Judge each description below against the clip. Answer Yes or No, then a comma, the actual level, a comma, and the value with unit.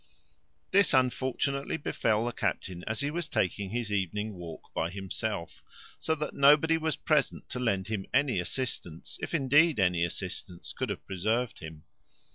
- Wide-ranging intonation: Yes, wide, 6.9 semitones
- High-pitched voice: No, low, 110 Hz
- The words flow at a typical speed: Yes, average, 155 wpm